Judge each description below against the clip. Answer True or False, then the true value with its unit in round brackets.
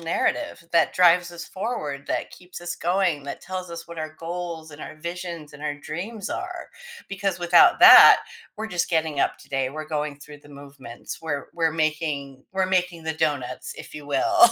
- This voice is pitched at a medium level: True (160 Hz)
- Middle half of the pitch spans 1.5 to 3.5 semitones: True (3.2 semitones)